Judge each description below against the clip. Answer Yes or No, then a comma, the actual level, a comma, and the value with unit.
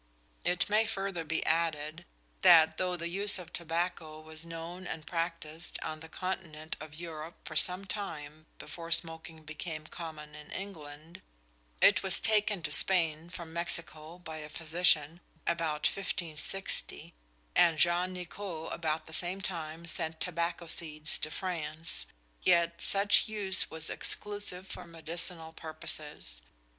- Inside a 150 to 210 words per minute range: No, slow, 135 wpm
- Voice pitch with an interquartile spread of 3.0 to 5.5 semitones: No, narrow, 2.4 semitones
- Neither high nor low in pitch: Yes, medium, 165 Hz